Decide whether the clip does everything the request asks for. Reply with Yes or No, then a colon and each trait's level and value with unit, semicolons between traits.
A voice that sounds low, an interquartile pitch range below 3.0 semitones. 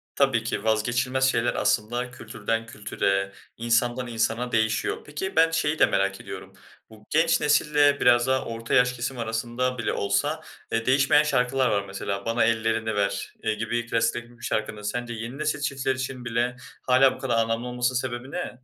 Yes: low, 120 Hz; narrow, 2.6 semitones